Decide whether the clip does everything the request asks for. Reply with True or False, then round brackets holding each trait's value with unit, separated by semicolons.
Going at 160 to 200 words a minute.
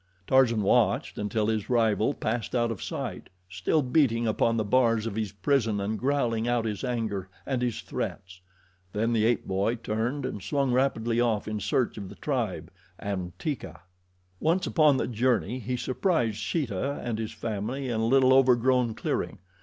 True (170 wpm)